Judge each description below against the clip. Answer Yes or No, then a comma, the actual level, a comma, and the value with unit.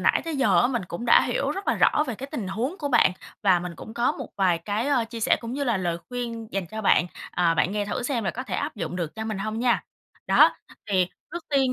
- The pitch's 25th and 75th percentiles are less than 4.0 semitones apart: No, average, 4.9 semitones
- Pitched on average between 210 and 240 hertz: Yes, high, 225 Hz